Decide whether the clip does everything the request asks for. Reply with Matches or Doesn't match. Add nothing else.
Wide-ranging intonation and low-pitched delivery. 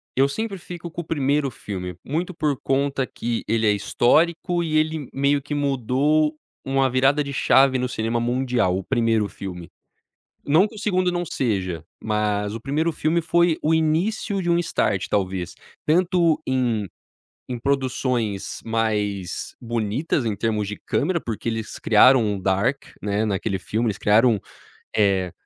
Matches